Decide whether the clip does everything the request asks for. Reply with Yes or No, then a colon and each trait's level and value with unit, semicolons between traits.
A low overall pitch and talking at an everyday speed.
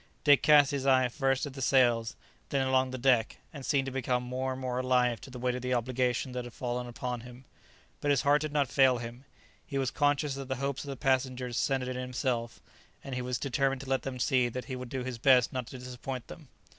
No: low, 130 Hz; fast, 245 wpm